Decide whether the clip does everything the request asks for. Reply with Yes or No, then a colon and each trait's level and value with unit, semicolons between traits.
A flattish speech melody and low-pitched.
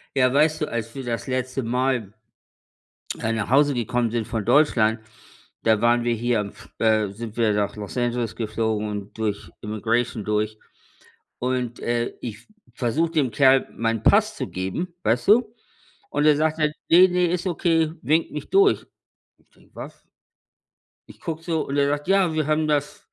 No: wide, 5.4 semitones; low, 125 Hz